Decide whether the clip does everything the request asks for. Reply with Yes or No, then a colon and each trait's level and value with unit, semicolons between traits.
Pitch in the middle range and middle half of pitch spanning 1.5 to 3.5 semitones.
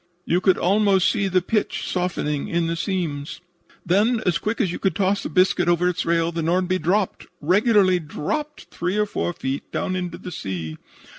Yes: medium, 180 Hz; average, 2.7 semitones